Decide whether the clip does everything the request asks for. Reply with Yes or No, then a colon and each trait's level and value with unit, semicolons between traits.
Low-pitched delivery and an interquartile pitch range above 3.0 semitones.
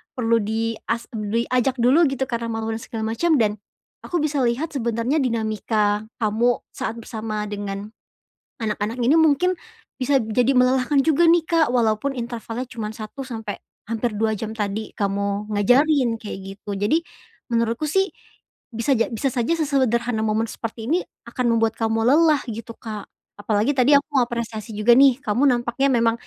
No: high, 230 Hz; average, 3.6 semitones